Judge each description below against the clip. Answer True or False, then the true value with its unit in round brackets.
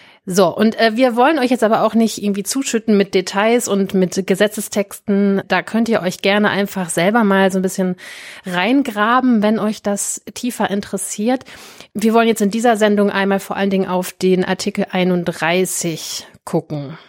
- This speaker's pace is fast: False (170 wpm)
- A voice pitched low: False (200 Hz)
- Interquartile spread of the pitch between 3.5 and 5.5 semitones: False (2.8 semitones)